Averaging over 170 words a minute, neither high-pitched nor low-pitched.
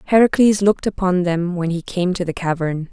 Yes: fast, 205 wpm; medium, 180 Hz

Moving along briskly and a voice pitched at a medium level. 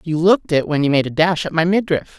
Yes: fast, 300 wpm; medium, 165 Hz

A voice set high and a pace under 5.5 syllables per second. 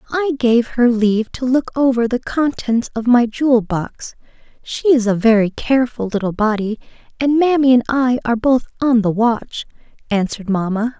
Yes: high, 240 Hz; 5.0 syllables/s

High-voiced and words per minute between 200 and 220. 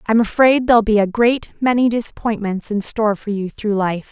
Yes: high, 220 Hz; fast, 205 wpm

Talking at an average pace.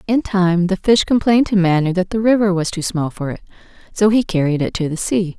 No: fast, 245 wpm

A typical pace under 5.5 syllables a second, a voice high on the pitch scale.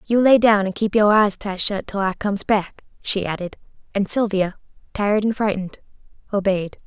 Yes: 5.3 syllables/s; high, 200 Hz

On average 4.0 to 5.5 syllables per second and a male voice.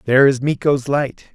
Yes: 5.0 syllables/s; male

